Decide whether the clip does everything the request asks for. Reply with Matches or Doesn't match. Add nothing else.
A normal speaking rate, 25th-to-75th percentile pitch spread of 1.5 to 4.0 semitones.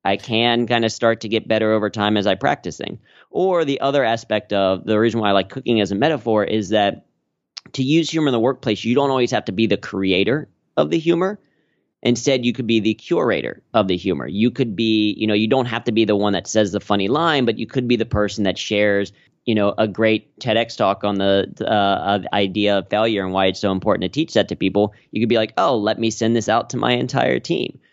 Doesn't match